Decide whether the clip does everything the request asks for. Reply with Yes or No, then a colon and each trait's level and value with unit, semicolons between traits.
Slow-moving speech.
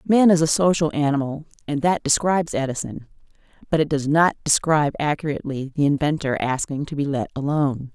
No: average, 165 wpm